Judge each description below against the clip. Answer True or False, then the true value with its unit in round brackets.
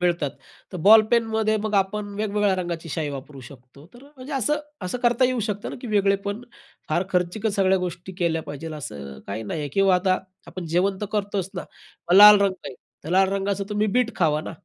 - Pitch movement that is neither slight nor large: True (4.0 semitones)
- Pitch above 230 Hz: False (195 Hz)